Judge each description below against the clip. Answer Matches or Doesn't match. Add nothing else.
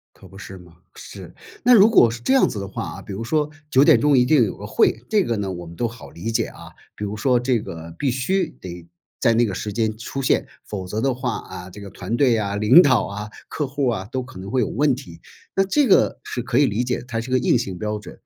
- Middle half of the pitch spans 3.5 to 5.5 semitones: Matches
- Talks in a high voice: Doesn't match